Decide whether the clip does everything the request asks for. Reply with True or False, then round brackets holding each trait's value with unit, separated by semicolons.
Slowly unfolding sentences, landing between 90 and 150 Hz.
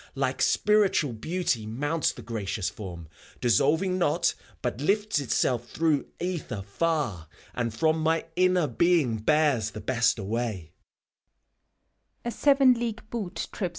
True (105 wpm; 135 Hz)